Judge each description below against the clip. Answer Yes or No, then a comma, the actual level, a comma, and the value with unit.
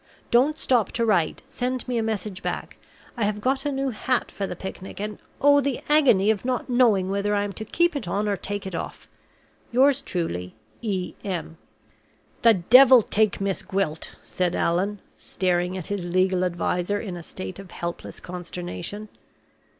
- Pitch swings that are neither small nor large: Yes, average, 4.9 semitones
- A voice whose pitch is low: No, high, 205 Hz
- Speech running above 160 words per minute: Yes, average, 175 wpm